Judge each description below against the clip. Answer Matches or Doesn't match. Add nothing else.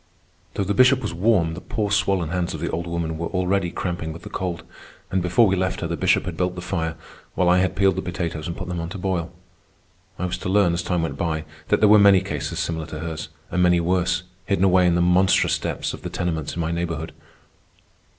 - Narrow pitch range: Matches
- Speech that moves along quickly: Matches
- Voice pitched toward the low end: Matches